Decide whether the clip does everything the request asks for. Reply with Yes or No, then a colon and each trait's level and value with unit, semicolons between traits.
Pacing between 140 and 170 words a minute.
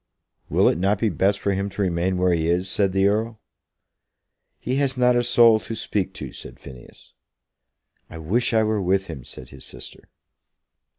No: average, 185 wpm